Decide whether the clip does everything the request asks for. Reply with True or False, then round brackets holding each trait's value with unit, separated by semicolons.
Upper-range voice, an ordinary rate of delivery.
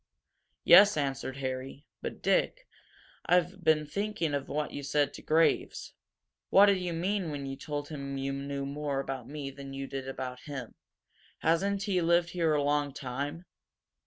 False (145 Hz; 165 wpm)